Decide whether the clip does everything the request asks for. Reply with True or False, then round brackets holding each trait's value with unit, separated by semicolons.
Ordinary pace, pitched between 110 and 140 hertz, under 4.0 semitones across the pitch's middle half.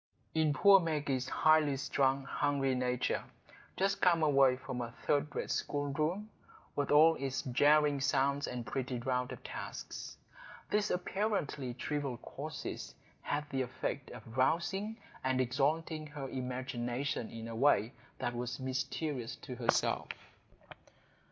False (125 wpm; 135 Hz; 3.2 semitones)